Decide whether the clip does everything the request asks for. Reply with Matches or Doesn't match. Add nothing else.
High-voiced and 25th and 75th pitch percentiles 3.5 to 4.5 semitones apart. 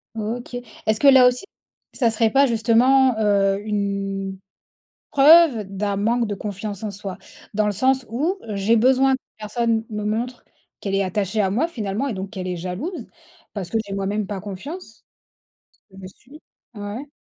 Matches